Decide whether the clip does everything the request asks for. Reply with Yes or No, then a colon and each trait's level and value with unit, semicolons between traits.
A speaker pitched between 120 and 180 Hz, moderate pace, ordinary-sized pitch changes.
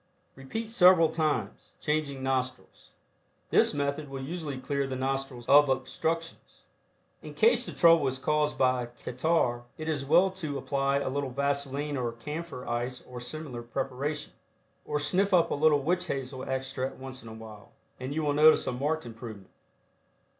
Yes: medium, 140 Hz; average, 160 wpm; average, 3.2 semitones